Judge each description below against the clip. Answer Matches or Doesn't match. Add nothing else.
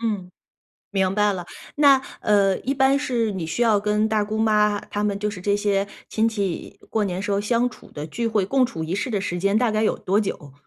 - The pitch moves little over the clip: Matches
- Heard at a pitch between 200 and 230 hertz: Matches